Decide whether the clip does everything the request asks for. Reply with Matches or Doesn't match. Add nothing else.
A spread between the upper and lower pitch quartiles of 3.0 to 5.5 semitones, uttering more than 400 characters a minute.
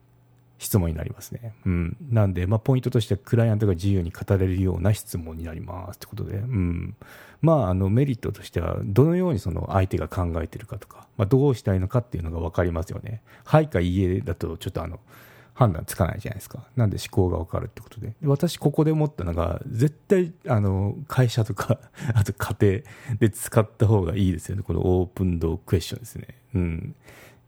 Matches